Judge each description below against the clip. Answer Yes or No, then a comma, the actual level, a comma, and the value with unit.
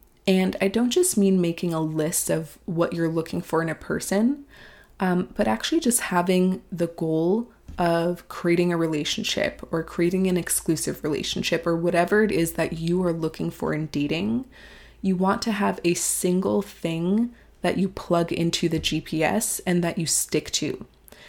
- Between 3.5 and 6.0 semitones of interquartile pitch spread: No, average, 2.7 semitones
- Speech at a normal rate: Yes, average, 170 wpm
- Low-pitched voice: No, medium, 175 Hz